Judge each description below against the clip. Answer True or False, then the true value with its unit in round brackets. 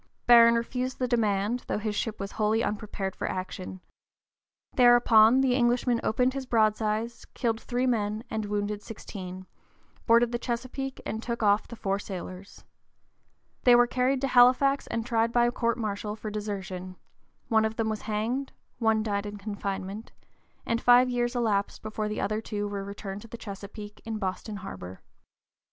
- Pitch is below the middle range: False (220 Hz)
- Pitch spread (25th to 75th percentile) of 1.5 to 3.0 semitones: True (2.7 semitones)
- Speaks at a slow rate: False (165 wpm)